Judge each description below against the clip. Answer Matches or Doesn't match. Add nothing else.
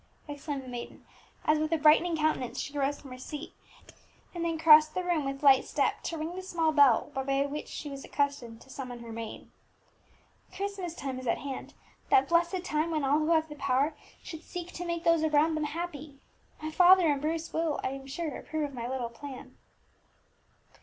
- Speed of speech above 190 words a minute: Matches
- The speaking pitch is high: Matches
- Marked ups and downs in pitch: Doesn't match